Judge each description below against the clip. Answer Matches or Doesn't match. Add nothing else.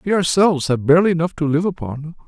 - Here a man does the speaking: Matches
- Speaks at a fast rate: Matches